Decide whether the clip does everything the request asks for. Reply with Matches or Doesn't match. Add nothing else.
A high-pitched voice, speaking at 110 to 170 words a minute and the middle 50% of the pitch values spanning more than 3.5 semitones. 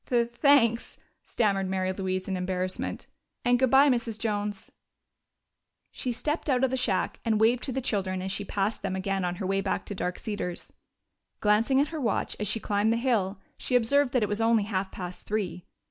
Doesn't match